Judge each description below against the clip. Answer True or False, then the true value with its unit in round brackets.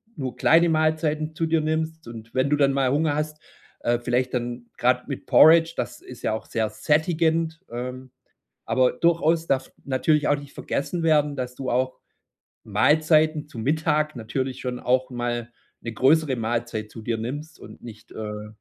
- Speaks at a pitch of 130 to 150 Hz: True (135 Hz)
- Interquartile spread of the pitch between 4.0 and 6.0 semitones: True (4.4 semitones)